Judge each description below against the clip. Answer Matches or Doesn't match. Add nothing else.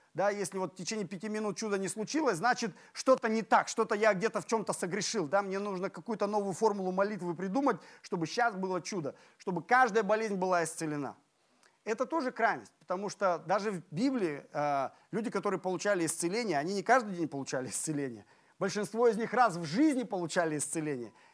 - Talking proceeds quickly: Matches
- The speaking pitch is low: Doesn't match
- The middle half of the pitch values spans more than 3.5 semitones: Matches